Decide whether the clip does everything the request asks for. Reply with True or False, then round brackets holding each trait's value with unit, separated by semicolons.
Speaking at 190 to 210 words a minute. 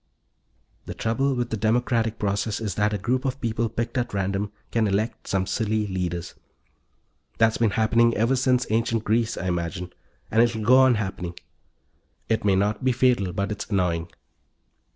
False (170 wpm)